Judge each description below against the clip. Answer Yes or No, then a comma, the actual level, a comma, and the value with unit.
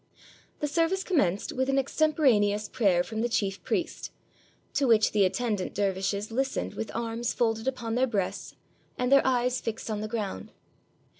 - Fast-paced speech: No, average, 165 wpm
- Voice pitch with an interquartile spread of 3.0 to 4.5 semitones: Yes, average, 4.2 semitones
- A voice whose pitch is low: No, high, 230 Hz